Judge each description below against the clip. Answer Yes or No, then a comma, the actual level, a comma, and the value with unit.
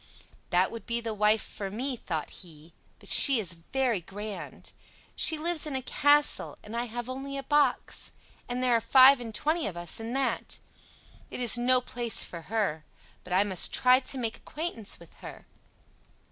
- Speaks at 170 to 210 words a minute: Yes, average, 185 wpm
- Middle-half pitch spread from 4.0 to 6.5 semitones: Yes, average, 4.6 semitones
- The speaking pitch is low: No, high, 235 Hz